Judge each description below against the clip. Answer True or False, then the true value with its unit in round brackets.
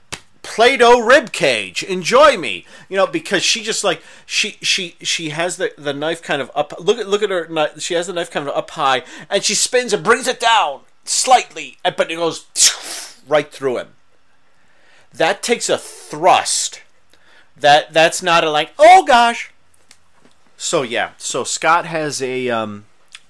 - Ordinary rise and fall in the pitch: False (6.6 semitones)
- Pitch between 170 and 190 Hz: True (185 Hz)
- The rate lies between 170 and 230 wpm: True (175 wpm)